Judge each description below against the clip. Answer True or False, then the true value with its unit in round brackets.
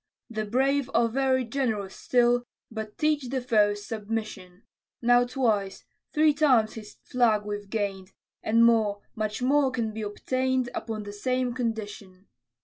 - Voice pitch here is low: False (225 Hz)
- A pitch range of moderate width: True (3.5 semitones)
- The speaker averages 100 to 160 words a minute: True (140 wpm)